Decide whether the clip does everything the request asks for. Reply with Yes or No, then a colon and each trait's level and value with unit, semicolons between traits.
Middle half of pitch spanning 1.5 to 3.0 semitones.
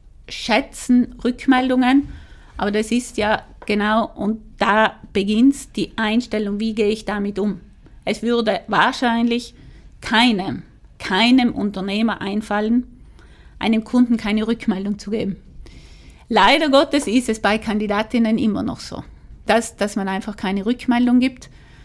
Yes: narrow, 2.6 semitones